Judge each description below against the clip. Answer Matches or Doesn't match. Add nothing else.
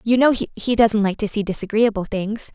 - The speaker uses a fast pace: Matches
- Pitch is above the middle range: Matches